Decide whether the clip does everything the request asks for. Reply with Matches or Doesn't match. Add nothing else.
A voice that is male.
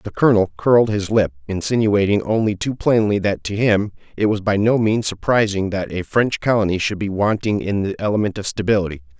Matches